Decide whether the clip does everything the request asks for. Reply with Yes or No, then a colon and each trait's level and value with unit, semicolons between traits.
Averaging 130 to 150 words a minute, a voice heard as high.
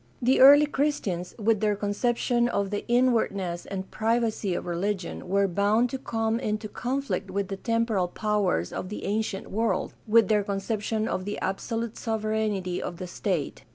No: average, 160 wpm; high, 210 Hz